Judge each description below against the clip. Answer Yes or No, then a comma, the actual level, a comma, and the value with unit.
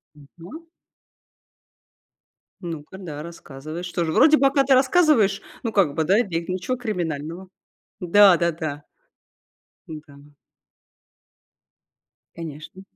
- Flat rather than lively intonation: No, average, 4.9 semitones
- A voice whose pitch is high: No, medium, 175 Hz